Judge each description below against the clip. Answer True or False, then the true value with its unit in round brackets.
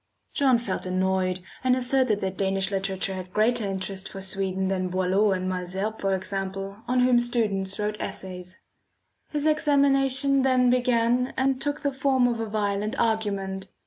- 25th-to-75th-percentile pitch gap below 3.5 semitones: False (4.8 semitones)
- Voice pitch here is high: True (205 Hz)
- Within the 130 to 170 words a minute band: True (155 wpm)